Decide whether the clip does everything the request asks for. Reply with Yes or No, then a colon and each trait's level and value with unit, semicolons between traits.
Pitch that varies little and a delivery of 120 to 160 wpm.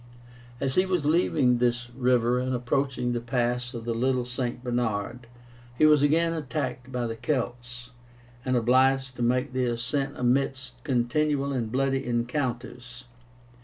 Yes: narrow, 1.8 semitones; average, 145 wpm